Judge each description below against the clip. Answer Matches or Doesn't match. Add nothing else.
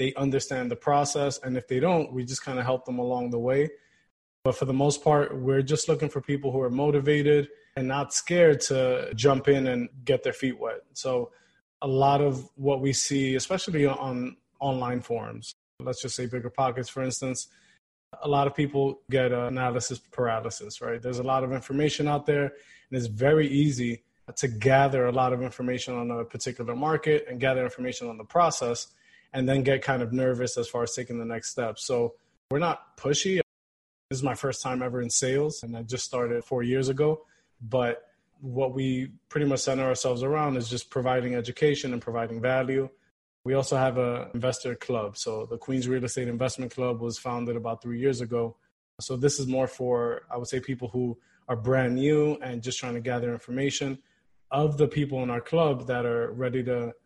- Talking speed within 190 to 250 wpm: Matches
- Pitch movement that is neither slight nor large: Doesn't match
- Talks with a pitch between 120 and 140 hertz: Matches